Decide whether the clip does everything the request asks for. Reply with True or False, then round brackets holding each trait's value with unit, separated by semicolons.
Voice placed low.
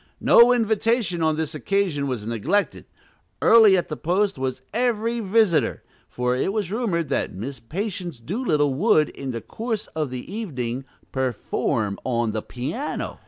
False (165 Hz)